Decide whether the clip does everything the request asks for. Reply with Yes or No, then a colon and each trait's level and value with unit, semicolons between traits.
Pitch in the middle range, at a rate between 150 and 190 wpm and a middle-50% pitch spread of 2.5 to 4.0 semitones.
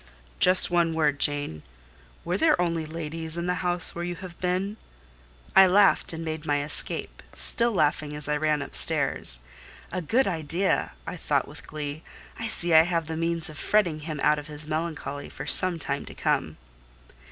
Yes: medium, 165 Hz; average, 180 wpm; average, 2.8 semitones